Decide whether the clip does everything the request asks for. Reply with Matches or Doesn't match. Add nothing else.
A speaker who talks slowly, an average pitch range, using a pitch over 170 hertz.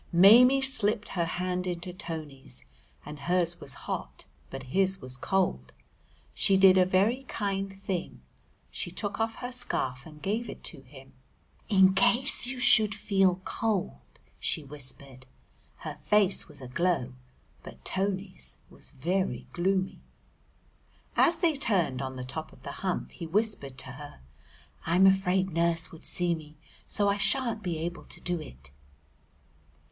Doesn't match